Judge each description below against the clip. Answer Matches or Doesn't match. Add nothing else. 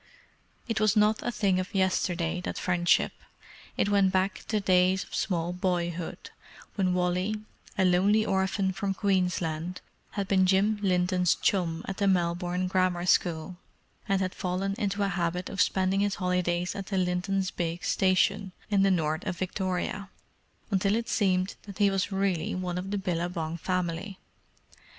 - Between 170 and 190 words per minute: Doesn't match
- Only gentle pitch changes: Matches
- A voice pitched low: Doesn't match